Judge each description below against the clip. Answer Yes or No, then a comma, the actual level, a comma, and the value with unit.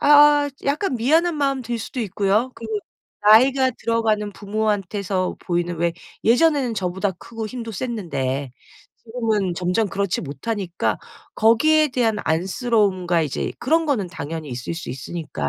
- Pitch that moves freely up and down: Yes, wide, 5.8 semitones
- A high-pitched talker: Yes, high, 215 Hz